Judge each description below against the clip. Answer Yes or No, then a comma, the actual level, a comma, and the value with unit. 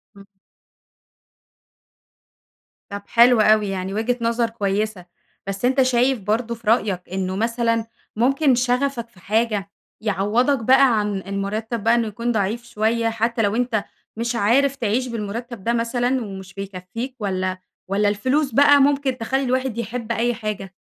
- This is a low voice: No, high, 230 Hz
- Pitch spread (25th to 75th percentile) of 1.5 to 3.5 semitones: Yes, average, 3.2 semitones